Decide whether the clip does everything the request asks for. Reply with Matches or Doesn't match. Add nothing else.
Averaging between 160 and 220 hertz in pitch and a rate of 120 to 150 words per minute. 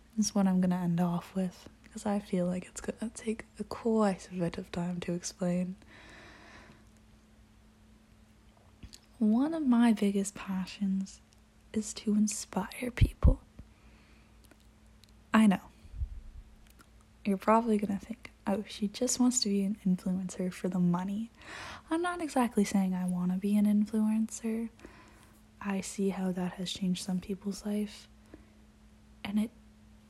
Matches